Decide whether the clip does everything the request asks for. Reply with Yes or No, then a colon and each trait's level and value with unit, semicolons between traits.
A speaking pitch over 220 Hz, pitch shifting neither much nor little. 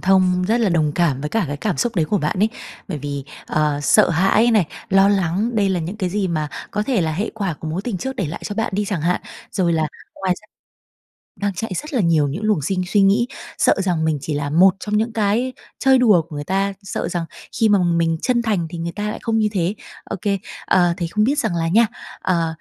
No: high, 190 Hz; average, 4.3 semitones